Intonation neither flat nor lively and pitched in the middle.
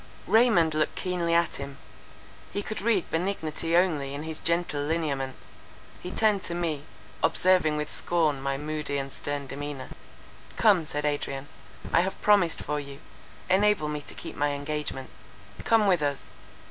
Yes: average, 3.9 semitones; medium, 155 Hz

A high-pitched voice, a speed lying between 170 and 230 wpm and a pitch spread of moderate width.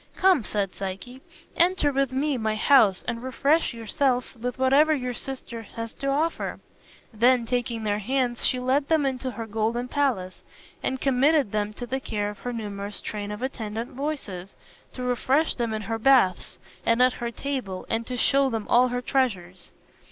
Yes: high, 245 Hz; average, 175 wpm; average, 3.7 semitones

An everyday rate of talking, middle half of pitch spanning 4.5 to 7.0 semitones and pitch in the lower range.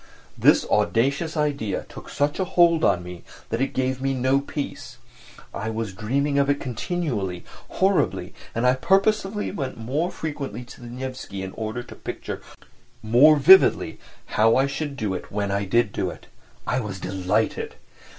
Yes: average, 165 wpm; average, 5.3 semitones; low, 130 Hz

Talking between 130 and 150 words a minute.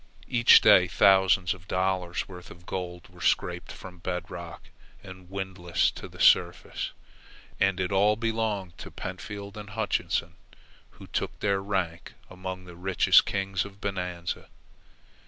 Yes: slow, 135 wpm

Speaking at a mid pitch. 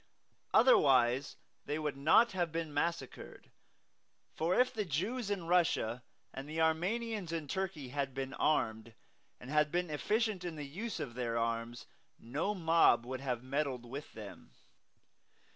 Yes: medium, 150 Hz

